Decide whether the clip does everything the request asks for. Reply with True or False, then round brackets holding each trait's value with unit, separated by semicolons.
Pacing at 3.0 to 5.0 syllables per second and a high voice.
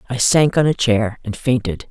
False (4.8 syllables/s; 120 Hz)